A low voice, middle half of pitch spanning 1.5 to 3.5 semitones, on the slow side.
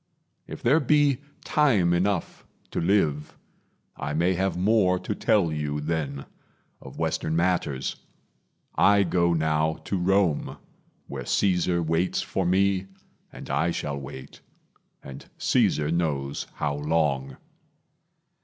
No: very low, 85 Hz; average, 4.3 semitones; slow, 120 wpm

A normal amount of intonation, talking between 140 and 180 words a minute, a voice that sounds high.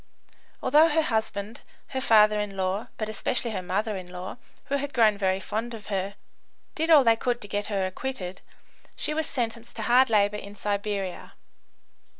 Yes: average, 3.3 semitones; average, 175 wpm; high, 215 Hz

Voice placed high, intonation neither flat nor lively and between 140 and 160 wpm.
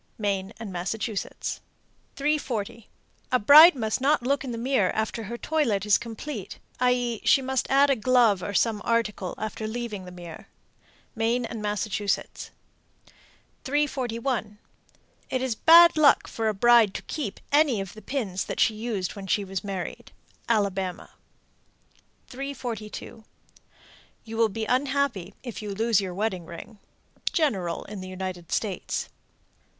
Yes: high, 225 Hz; average, 4.1 semitones; average, 145 wpm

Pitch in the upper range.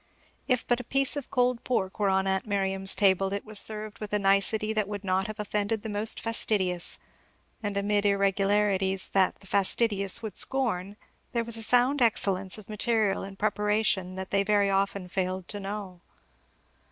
Yes: high, 205 Hz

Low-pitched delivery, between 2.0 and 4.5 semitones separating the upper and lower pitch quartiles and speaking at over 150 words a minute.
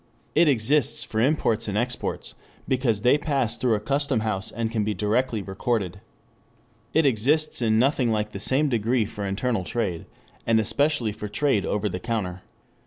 Yes: low, 115 Hz; average, 3.9 semitones; average, 170 wpm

